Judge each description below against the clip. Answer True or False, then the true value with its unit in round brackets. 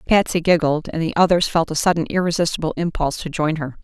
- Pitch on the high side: False (165 Hz)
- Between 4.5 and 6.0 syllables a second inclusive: False (6.4 syllables/s)